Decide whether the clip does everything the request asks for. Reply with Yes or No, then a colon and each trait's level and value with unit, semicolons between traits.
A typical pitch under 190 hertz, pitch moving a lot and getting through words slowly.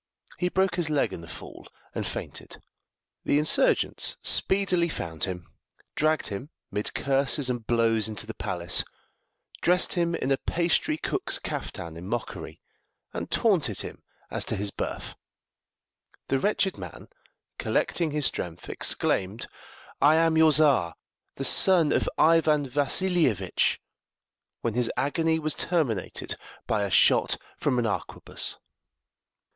Yes: medium, 140 Hz; wide, 7.1 semitones; slow, 130 wpm